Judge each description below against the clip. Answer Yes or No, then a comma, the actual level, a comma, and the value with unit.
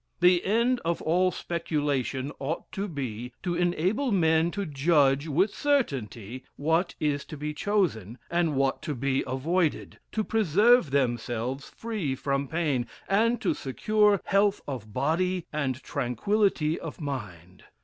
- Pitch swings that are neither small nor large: No, wide, 5.7 semitones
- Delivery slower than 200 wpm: Yes, average, 140 wpm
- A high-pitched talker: No, medium, 155 Hz